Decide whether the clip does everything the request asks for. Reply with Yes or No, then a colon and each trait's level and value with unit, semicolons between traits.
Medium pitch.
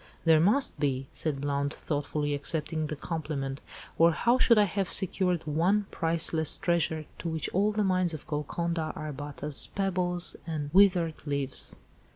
Yes: medium, 160 Hz